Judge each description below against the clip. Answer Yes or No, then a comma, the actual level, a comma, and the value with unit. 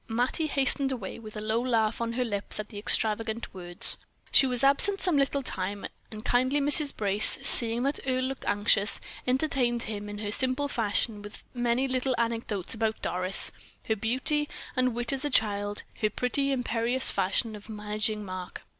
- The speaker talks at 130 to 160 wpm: No, average, 175 wpm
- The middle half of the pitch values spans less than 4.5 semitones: Yes, average, 3.7 semitones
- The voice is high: Yes, high, 230 Hz